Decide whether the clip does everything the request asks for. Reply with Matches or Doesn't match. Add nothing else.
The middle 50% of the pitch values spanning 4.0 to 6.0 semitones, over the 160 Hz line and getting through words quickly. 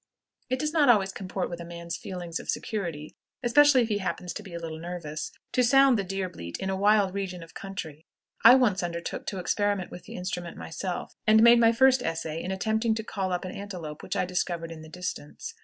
Matches